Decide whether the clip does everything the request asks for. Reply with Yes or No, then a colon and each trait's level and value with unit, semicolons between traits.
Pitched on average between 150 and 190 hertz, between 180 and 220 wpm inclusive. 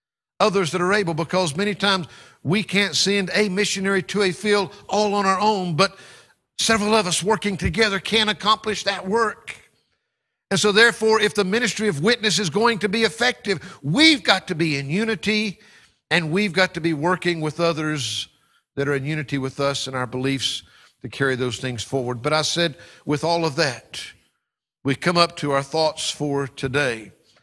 Yes: medium, 185 Hz; average, 185 wpm